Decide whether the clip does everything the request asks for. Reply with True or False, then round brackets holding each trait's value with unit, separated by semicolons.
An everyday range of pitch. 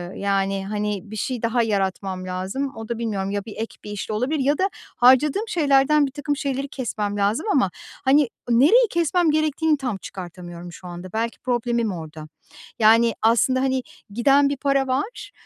False (5.7 semitones)